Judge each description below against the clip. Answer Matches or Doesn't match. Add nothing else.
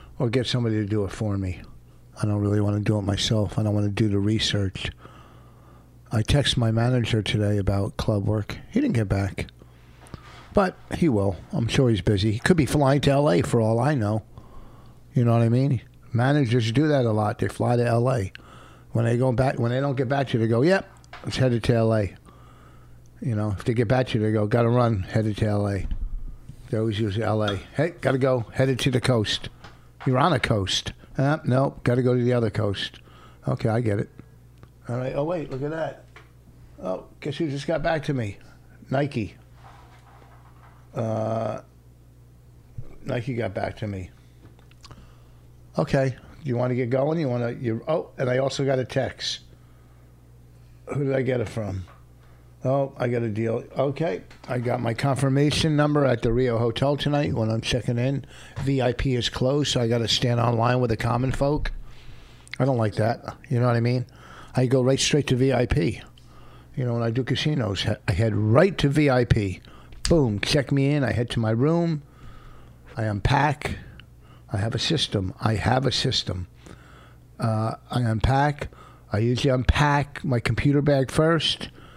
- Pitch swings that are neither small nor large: Matches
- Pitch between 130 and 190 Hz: Doesn't match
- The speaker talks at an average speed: Matches